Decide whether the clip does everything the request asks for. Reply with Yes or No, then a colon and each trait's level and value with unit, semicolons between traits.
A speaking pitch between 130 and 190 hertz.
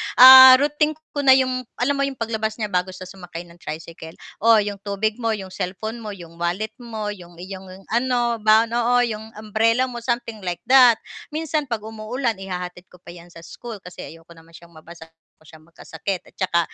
No: high, 215 Hz